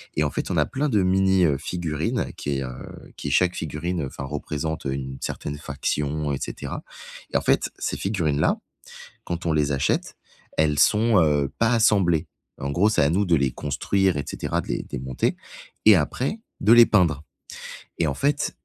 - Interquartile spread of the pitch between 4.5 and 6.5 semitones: Yes, average, 5.0 semitones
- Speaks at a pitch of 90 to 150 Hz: No, very low, 80 Hz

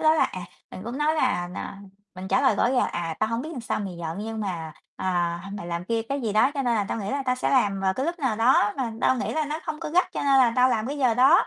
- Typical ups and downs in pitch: No, wide, 5.8 semitones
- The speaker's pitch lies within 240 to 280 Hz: No, high, 230 Hz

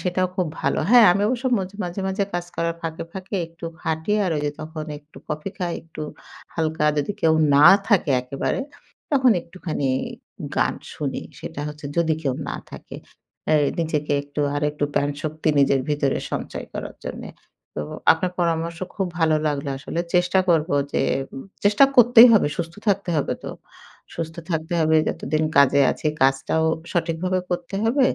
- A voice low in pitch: No, medium, 165 Hz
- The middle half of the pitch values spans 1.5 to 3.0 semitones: No, average, 3.4 semitones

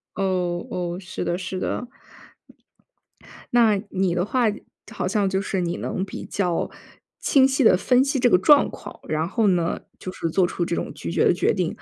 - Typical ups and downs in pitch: Yes, average, 4.0 semitones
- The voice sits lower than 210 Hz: Yes, high, 190 Hz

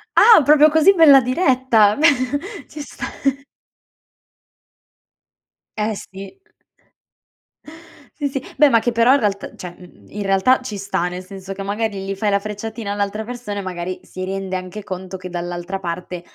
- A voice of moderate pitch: No, high, 205 Hz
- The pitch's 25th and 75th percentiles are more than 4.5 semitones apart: Yes, average, 4.9 semitones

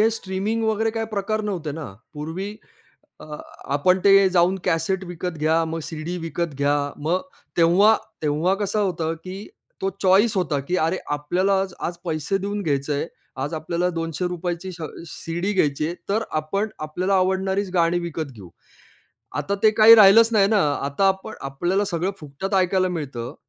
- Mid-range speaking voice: Yes, medium, 180 Hz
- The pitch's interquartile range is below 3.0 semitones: No, average, 3.5 semitones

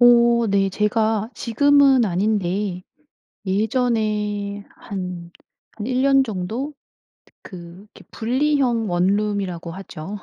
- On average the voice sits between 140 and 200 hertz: No, high, 210 Hz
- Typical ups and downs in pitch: Yes, average, 3.9 semitones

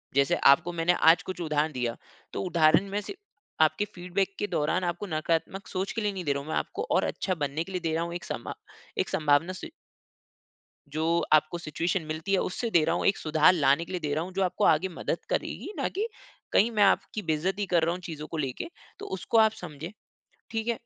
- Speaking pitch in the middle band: Yes, medium, 170 Hz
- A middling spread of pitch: Yes, average, 3.7 semitones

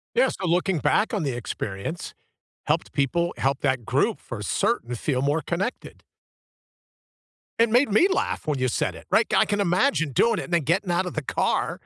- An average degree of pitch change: No, wide, 6.6 semitones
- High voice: No, medium, 170 Hz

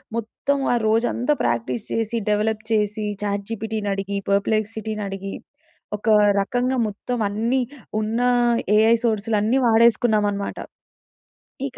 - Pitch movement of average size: No, narrow, 2.2 semitones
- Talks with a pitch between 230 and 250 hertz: No, high, 220 Hz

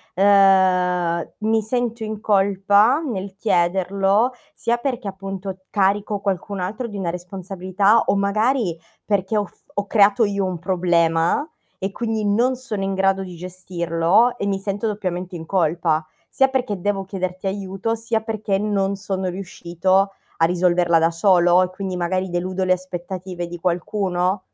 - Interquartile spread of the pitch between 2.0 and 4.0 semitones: Yes, narrow, 2.4 semitones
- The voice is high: Yes, high, 195 Hz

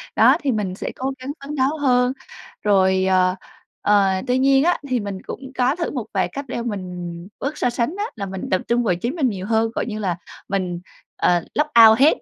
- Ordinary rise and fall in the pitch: No, wide, 6.0 semitones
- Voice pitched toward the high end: Yes, high, 230 Hz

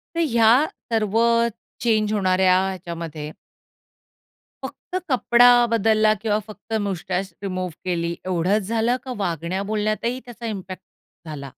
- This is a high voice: Yes, high, 200 Hz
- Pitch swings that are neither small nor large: Yes, average, 3.7 semitones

